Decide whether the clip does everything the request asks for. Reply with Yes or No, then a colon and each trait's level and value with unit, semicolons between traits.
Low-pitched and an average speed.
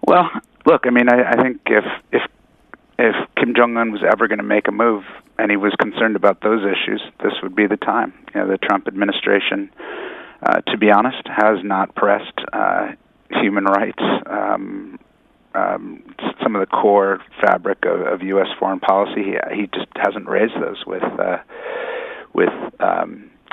No: very high, 295 Hz; average, 180 wpm